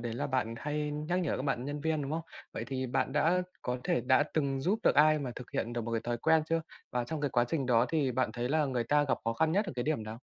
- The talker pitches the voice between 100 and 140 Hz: Yes, low, 135 Hz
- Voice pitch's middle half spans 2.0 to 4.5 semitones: Yes, average, 4.1 semitones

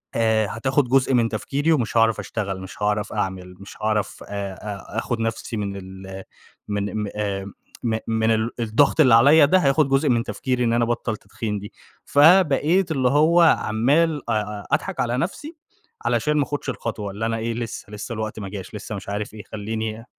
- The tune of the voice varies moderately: Yes, average, 4.5 semitones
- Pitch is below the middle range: Yes, low, 115 Hz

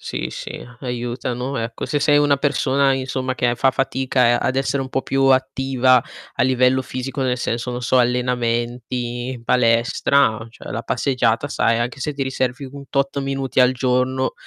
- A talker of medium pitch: No, low, 130 Hz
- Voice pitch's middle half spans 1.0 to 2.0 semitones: Yes, narrow, 1.7 semitones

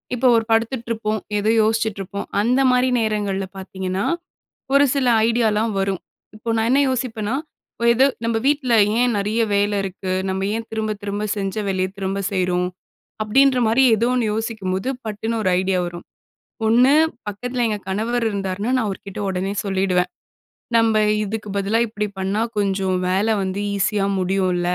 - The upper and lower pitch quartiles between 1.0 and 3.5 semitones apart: Yes, average, 3.0 semitones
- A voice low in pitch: No, high, 210 Hz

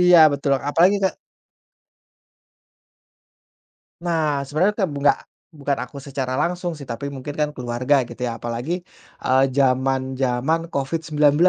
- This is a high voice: No, medium, 140 Hz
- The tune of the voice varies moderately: Yes, average, 3.7 semitones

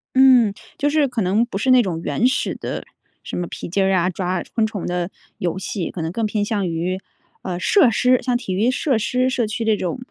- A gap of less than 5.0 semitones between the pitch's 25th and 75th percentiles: No, wide, 5.4 semitones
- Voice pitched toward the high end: Yes, high, 210 Hz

